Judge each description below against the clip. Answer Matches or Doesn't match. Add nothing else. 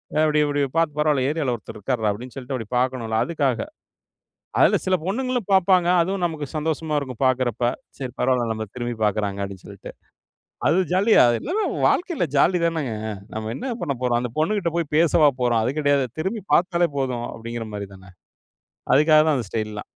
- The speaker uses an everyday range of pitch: Doesn't match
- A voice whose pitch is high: Doesn't match